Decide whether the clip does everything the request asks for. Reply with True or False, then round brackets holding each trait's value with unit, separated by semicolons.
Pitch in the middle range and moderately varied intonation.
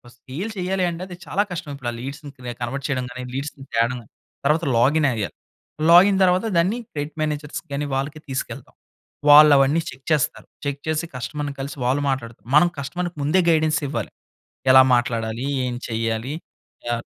True (145 Hz; 3.8 semitones)